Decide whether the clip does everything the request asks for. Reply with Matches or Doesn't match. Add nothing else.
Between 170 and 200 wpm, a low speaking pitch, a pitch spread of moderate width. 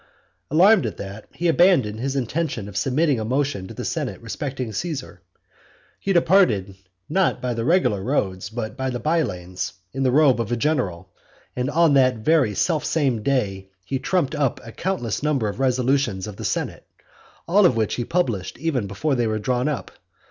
Doesn't match